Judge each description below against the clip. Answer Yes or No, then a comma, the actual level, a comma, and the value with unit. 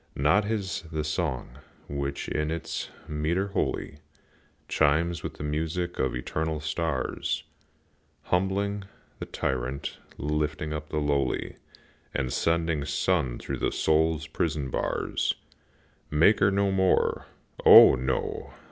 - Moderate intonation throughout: Yes, average, 3.1 semitones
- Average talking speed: No, slow, 120 wpm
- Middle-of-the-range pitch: No, very low, 80 Hz